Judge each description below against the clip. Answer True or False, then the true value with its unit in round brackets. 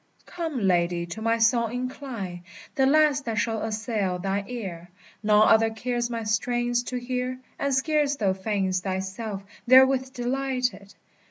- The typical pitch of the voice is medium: False (230 Hz)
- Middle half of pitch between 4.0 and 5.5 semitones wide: True (4.4 semitones)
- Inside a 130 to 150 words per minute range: True (145 wpm)